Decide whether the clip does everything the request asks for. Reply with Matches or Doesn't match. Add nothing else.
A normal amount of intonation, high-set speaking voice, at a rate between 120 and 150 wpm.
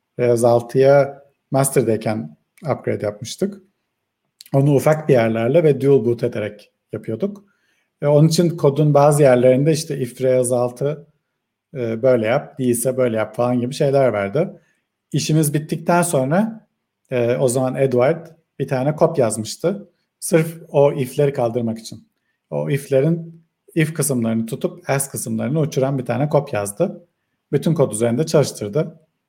Doesn't match